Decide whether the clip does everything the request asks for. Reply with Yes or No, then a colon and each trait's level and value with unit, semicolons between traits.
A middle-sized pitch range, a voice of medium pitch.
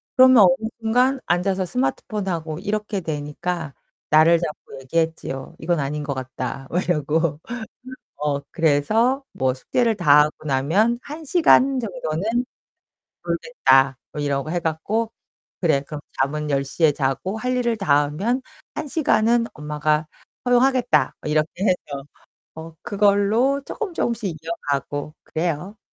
No: wide, 7.0 semitones; medium, 170 Hz